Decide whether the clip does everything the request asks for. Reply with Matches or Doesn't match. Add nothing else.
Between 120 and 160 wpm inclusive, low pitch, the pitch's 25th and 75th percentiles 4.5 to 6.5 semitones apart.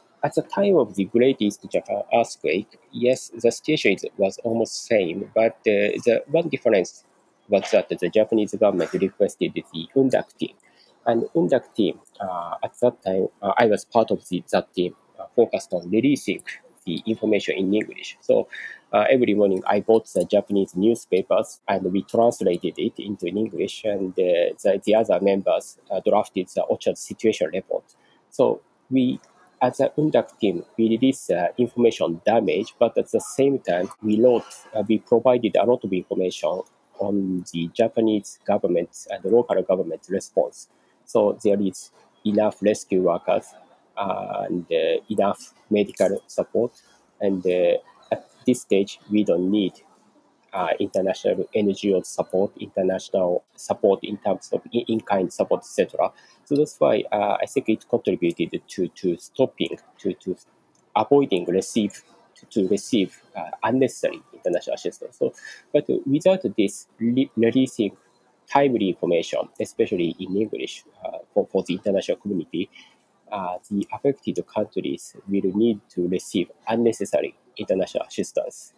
Matches